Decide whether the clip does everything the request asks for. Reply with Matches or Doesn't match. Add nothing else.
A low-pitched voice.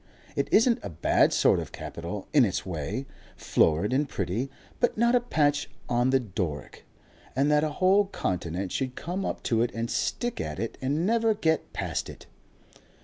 Matches